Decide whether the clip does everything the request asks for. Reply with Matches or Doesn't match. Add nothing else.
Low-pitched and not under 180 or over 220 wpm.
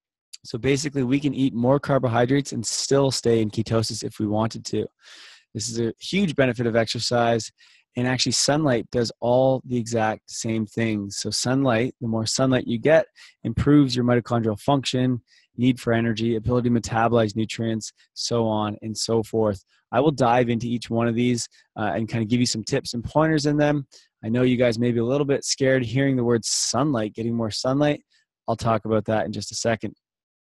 Matches